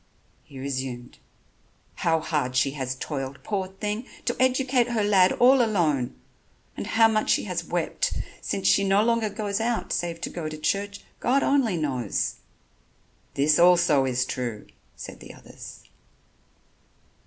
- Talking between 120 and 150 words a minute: Yes, average, 145 wpm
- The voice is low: No, medium, 180 Hz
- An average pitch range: No, wide, 8.2 semitones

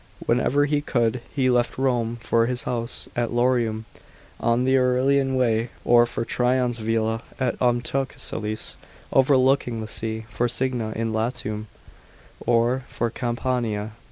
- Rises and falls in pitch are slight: Yes, narrow, 2.1 semitones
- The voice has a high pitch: No, low, 120 Hz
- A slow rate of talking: Yes, slow, 130 wpm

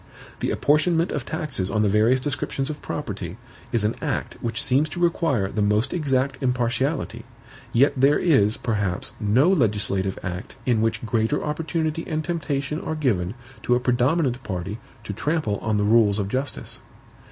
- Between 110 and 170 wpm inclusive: Yes, average, 165 wpm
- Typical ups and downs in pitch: No, wide, 5.9 semitones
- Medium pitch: No, low, 125 Hz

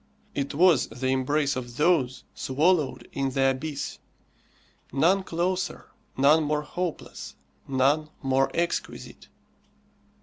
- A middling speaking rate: No, slow, 105 wpm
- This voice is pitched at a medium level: Yes, medium, 145 Hz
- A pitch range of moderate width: Yes, average, 3.9 semitones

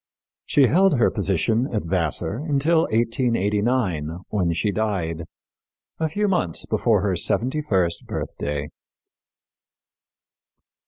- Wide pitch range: Yes, wide, 7.0 semitones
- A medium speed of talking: No, slow, 105 wpm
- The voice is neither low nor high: No, low, 105 Hz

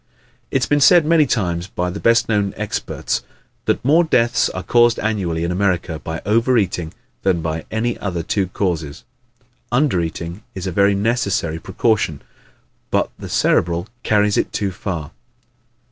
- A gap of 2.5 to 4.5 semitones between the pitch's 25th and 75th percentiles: No, average, 5.2 semitones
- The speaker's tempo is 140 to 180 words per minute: Yes, average, 160 wpm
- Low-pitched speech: Yes, low, 100 Hz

